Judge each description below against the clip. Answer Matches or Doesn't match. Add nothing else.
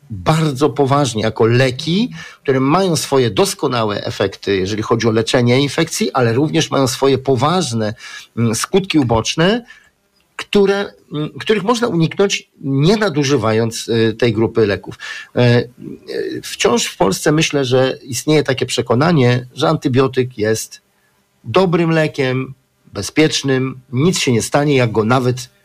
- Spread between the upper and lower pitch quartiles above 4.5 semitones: Matches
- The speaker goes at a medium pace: Matches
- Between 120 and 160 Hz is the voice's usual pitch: Matches